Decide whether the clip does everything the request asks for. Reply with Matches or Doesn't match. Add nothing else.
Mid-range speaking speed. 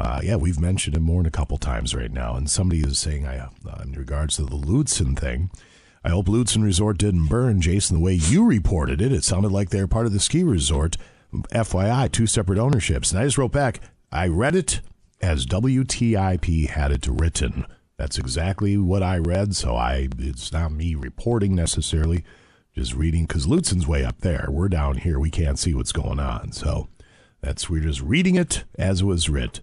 Doesn't match